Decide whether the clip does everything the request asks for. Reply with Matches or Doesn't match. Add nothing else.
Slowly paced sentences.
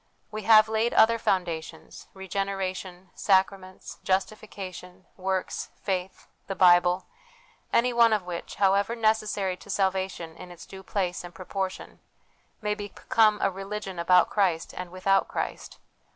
Matches